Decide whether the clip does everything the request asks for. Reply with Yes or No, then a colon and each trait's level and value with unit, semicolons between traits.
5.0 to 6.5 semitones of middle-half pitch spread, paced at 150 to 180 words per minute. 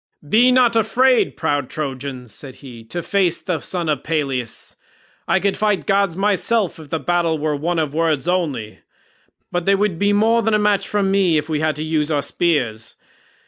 No: average, 5.3 semitones; average, 190 wpm